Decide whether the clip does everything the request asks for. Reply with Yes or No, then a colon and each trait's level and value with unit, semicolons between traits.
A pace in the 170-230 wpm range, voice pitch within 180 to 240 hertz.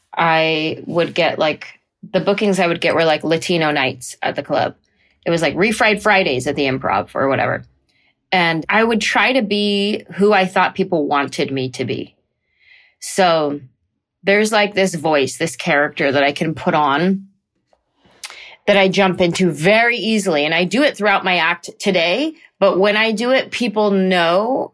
Yes: average, 175 wpm; medium, 185 Hz